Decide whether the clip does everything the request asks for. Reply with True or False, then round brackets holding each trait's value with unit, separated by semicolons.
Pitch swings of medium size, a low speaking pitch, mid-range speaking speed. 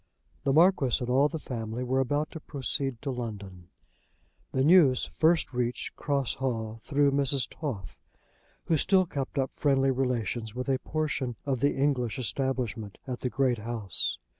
True (3.0 semitones; 130 Hz; 160 wpm)